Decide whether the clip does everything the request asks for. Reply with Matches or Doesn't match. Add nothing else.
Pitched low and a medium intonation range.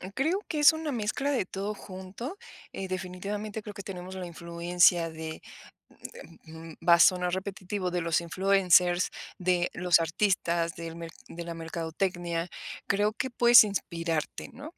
Doesn't match